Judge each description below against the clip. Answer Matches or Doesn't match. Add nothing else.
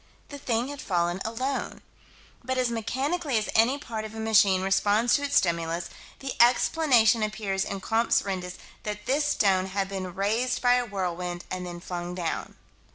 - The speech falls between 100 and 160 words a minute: Doesn't match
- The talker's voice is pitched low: Doesn't match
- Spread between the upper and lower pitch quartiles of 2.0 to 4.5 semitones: Doesn't match